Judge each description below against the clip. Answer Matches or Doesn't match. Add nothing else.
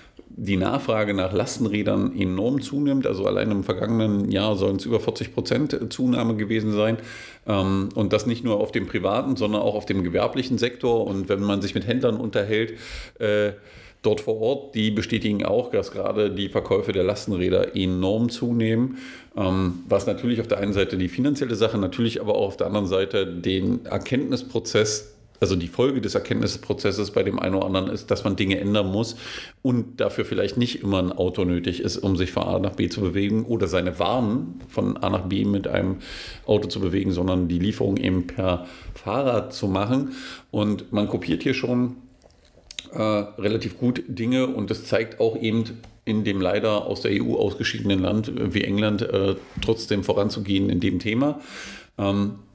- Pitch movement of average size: Matches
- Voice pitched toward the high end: Doesn't match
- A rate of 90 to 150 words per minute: Doesn't match